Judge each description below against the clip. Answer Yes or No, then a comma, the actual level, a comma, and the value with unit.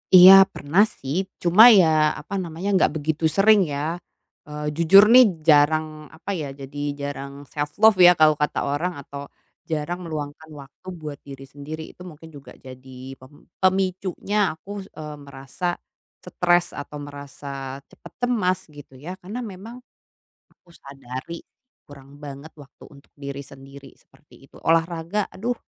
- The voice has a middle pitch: Yes, medium, 155 Hz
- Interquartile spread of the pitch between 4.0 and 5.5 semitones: Yes, average, 4.3 semitones